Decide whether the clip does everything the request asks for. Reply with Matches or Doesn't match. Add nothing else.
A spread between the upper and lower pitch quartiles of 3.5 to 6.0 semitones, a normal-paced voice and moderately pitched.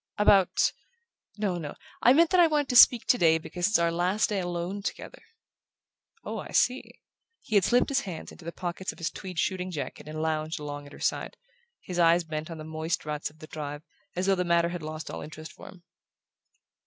Doesn't match